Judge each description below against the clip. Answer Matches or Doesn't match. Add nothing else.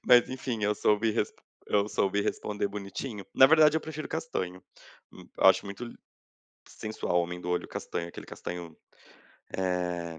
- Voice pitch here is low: Matches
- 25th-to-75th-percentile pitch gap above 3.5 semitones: Matches